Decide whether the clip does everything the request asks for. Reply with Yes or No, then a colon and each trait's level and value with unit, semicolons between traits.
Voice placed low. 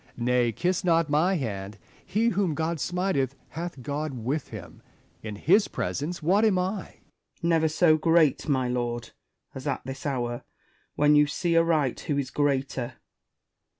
No: medium, 150 Hz